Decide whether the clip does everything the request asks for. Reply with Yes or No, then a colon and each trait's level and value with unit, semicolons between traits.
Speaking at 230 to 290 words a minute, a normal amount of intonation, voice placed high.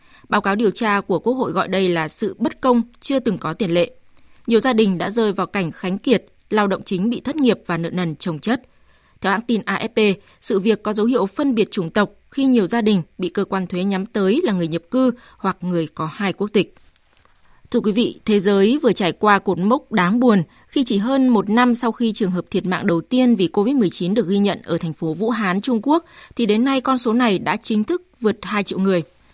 Yes: fast, 250 wpm; average, 4.1 semitones; high, 205 Hz